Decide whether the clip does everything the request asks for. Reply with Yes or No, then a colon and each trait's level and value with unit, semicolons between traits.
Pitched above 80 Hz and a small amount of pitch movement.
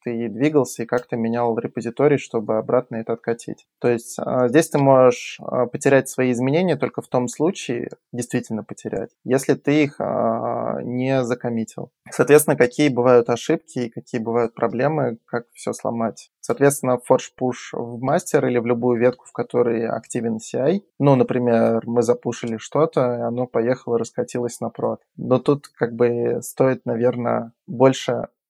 Yes: low, 125 Hz; narrow, 2.1 semitones